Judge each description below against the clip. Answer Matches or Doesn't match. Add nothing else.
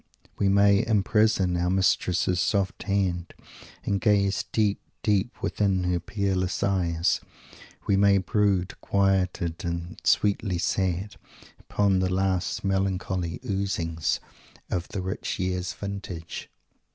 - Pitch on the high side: Doesn't match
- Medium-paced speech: Doesn't match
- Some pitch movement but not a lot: Doesn't match